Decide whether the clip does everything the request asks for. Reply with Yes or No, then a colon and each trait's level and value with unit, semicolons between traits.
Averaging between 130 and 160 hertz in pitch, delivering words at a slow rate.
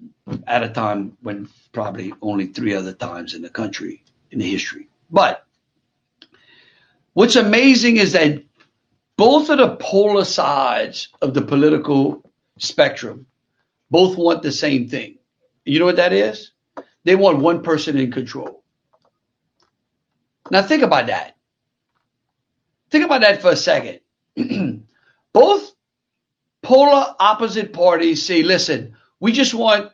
No: medium, 175 Hz; slow, 130 wpm